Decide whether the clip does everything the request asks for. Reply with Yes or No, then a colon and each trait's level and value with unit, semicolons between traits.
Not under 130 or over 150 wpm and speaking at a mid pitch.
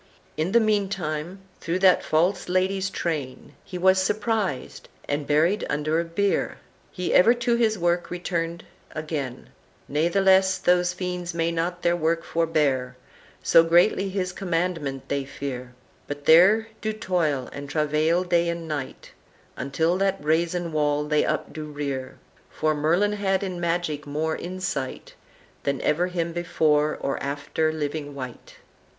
Yes: average, 145 wpm; medium, 170 Hz